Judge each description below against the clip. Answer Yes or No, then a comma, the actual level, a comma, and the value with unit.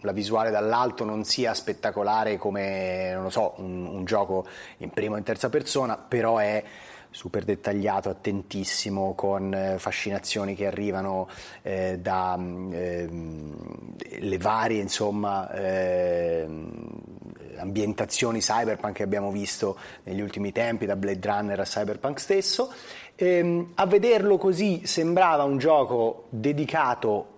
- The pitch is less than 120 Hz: Yes, low, 105 Hz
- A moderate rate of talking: Yes, average, 125 wpm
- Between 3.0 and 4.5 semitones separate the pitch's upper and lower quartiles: Yes, average, 3.5 semitones